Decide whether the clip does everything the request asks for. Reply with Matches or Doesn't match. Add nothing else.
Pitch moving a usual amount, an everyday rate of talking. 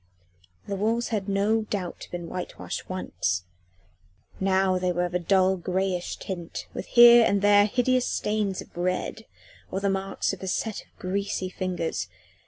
Doesn't match